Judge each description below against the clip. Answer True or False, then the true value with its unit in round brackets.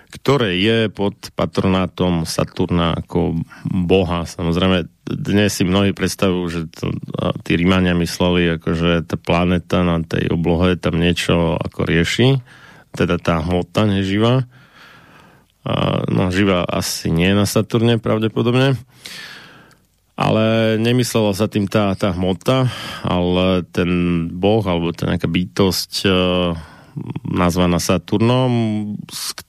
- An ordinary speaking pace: True (120 wpm)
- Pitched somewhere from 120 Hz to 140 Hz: False (95 Hz)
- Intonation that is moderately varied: True (3.5 semitones)